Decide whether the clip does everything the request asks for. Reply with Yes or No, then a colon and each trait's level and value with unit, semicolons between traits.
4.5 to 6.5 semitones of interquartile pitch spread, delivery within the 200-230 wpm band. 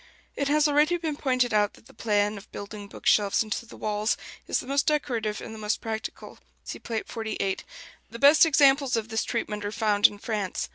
Yes: average, 4.8 semitones; fast, 205 wpm